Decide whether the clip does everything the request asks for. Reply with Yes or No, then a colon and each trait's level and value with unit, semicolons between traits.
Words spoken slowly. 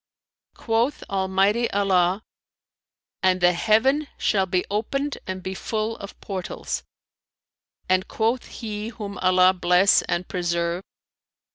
Yes: slow, 115 wpm